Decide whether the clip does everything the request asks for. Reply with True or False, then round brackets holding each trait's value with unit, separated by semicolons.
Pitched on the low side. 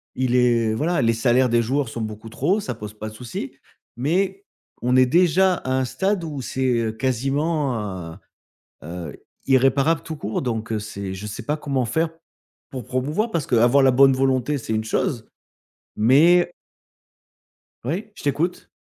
True (130 Hz)